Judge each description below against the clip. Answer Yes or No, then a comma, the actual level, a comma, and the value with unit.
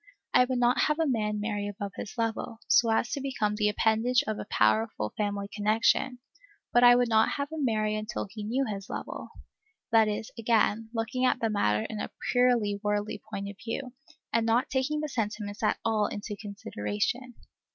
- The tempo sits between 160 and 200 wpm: Yes, average, 190 wpm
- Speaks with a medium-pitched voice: No, high, 220 Hz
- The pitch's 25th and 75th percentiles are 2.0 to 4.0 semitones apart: Yes, average, 2.9 semitones